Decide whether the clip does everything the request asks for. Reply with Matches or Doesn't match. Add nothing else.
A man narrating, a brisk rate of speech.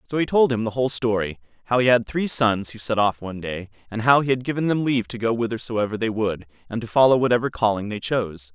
Matches